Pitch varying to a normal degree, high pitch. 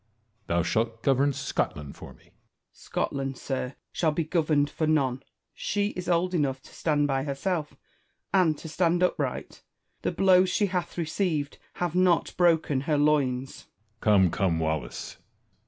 No: average, 4.7 semitones; medium, 150 Hz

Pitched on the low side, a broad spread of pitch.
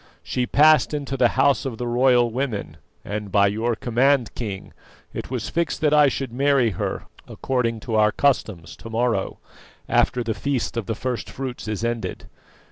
No: low, 120 Hz; average, 3.3 semitones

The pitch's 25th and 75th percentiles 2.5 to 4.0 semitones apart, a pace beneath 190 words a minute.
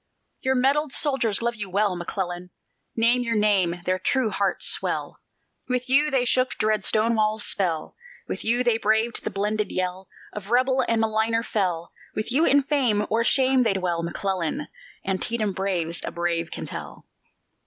No: average, 4.5 semitones; average, 165 wpm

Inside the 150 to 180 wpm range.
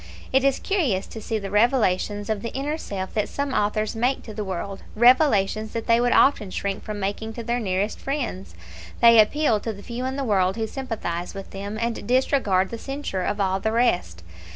No: fast, 205 wpm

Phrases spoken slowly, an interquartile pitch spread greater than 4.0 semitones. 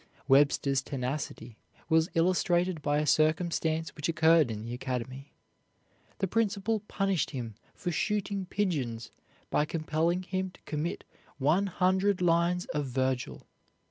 Yes: slow, 125 wpm; average, 5.0 semitones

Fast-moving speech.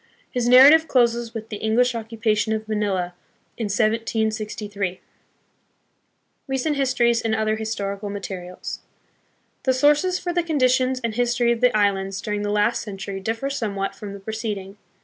No: average, 150 wpm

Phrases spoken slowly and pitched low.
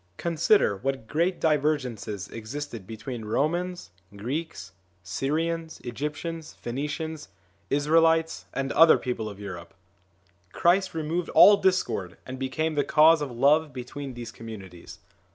No: slow, 120 wpm; medium, 145 Hz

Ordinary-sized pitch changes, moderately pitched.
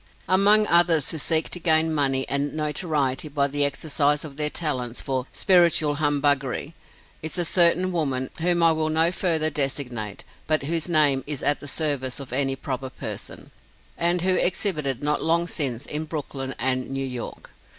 Yes: average, 3.4 semitones; medium, 150 Hz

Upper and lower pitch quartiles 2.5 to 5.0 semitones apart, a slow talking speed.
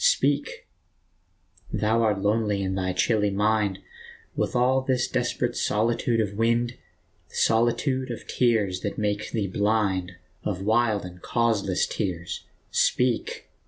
Yes: average, 3.1 semitones; slow, 125 wpm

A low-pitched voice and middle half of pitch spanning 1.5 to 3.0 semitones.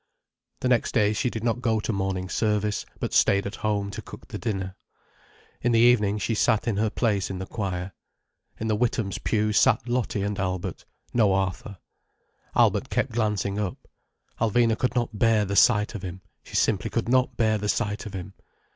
Yes: low, 105 Hz; narrow, 2.6 semitones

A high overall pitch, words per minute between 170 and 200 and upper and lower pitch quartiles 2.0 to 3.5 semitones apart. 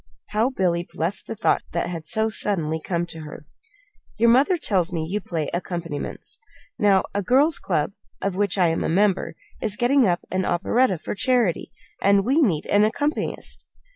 No: high, 195 Hz; average, 175 wpm; average, 4.5 semitones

